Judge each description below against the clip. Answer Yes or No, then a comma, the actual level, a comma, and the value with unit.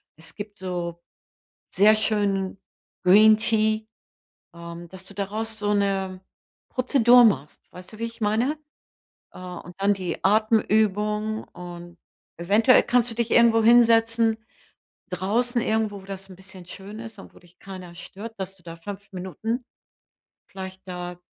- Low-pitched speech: No, high, 205 Hz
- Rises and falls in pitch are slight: No, average, 3.2 semitones